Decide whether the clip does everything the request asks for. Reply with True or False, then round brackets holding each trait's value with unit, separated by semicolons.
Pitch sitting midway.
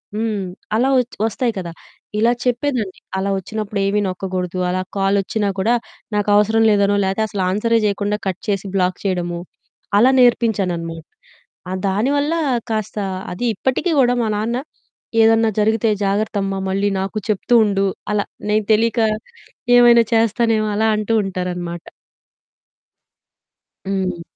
False (210 Hz)